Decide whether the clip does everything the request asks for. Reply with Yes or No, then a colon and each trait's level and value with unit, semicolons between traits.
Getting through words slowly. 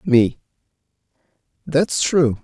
Yes: slow, 75 wpm